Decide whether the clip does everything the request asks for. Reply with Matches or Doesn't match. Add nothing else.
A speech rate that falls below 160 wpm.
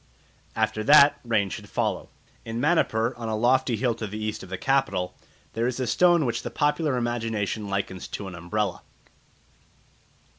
Doesn't match